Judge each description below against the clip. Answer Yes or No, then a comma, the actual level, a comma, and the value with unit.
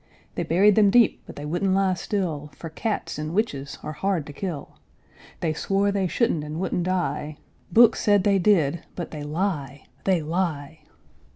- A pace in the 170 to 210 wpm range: Yes, average, 175 wpm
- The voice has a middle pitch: Yes, medium, 175 Hz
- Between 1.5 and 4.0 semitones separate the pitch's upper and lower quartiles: No, average, 4.6 semitones